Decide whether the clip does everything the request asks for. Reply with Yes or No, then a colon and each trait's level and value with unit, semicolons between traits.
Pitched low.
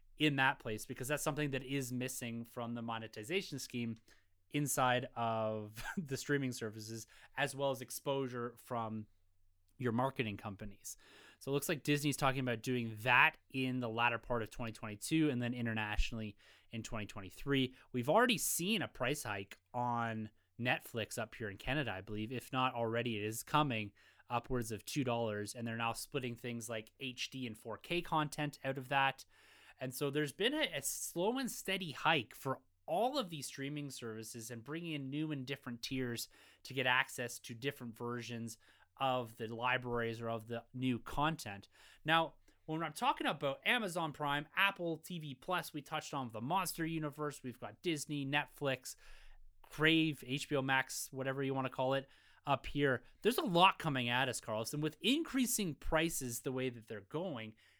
Yes: low, 130 Hz